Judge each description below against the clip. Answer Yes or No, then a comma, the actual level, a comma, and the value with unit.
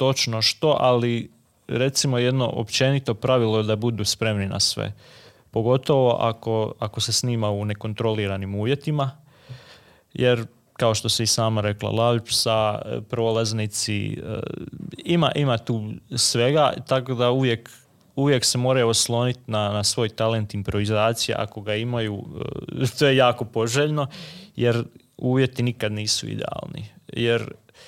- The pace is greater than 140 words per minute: No, average, 125 wpm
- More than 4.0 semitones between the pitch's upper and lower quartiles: No, average, 2.9 semitones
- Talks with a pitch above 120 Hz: No, low, 115 Hz